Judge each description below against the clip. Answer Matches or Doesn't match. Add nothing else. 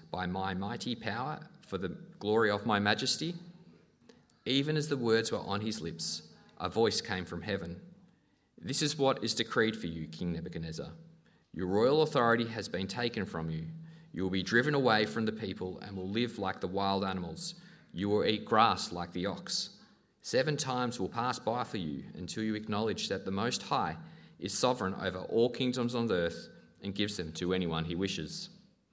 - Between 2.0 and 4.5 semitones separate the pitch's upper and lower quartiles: Doesn't match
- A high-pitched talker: Doesn't match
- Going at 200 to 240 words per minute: Doesn't match